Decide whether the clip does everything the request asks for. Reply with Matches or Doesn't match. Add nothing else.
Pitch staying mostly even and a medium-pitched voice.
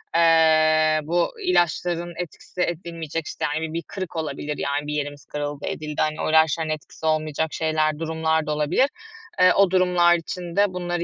Matches